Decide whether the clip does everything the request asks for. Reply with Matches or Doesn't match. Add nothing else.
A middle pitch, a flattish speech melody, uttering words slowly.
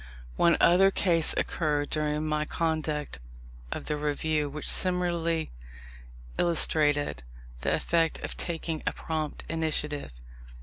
Matches